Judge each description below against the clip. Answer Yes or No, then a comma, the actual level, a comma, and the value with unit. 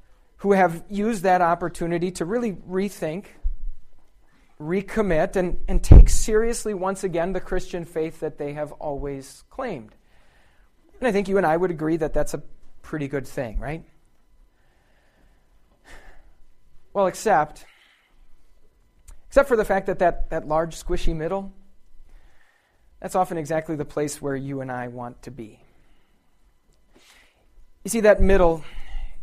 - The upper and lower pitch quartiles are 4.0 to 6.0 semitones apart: Yes, average, 5.1 semitones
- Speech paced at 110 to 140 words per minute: Yes, slow, 135 wpm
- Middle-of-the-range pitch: Yes, medium, 165 Hz